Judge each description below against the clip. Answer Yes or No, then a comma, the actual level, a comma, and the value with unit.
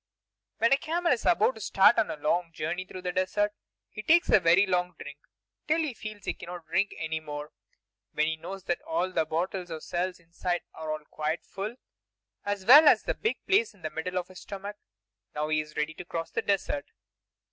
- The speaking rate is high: Yes, fast, 210 wpm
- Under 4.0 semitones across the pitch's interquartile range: No, average, 4.4 semitones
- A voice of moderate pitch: Yes, medium, 180 Hz